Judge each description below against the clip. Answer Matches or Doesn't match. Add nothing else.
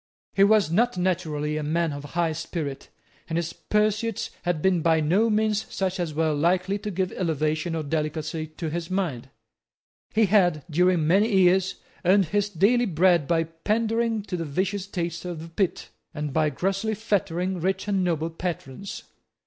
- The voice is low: Doesn't match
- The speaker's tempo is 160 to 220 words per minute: Matches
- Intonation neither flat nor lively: Matches